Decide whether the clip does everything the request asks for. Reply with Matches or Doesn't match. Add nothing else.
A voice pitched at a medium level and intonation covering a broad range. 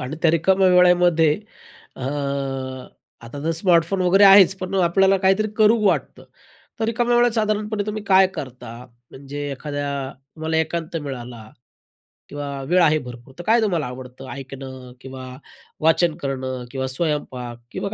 Matches